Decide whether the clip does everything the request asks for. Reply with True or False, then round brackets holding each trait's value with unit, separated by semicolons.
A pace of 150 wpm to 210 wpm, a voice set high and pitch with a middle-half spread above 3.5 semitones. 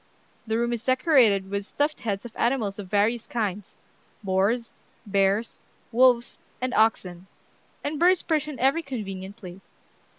False (140 wpm; 225 Hz; 4.6 semitones)